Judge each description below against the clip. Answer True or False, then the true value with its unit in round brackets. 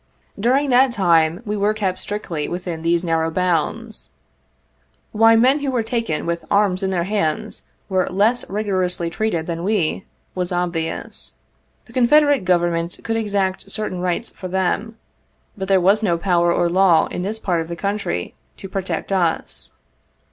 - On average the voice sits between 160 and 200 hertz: True (190 Hz)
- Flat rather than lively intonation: False (3.9 semitones)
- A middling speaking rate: True (160 wpm)